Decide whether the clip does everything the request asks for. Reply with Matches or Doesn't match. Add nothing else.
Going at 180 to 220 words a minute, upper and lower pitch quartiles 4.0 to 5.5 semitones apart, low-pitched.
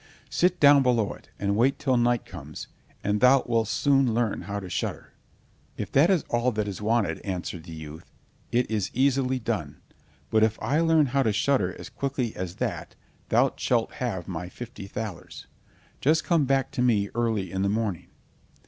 Matches